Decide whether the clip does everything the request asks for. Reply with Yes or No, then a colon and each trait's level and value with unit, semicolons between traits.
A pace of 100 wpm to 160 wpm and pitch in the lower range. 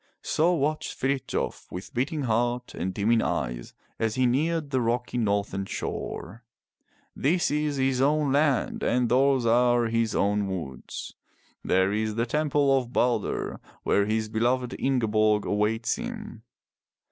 Yes: slow, 135 wpm; low, 120 Hz